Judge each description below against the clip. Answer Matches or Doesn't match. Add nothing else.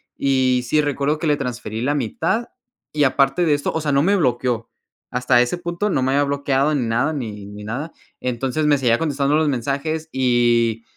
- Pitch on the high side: Doesn't match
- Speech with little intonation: Doesn't match